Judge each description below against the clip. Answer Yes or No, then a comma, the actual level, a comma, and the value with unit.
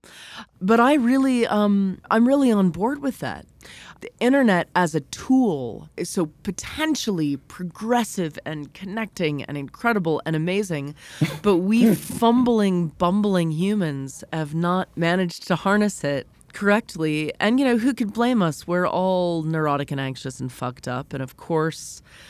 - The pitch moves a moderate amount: No, wide, 6.4 semitones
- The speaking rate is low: No, average, 150 wpm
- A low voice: No, medium, 180 Hz